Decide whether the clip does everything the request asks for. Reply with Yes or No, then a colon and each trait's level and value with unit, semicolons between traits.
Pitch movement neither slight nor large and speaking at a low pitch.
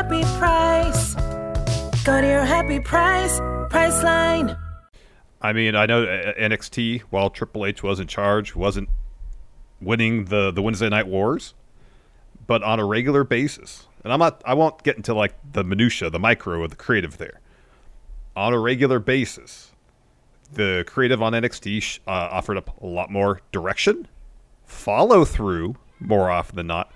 Yes: average, 4.4 semitones; low, 110 Hz